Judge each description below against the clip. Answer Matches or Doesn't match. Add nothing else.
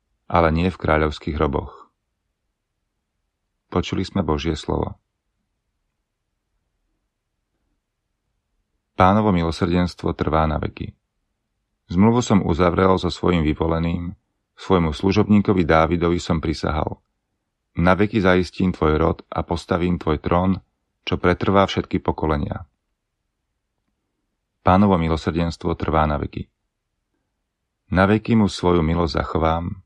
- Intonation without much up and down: Doesn't match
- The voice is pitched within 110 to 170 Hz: Doesn't match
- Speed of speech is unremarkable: Doesn't match